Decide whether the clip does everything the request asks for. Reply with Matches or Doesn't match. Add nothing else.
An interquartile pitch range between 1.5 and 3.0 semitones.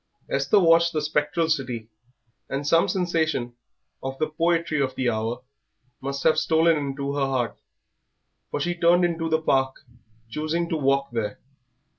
Doesn't match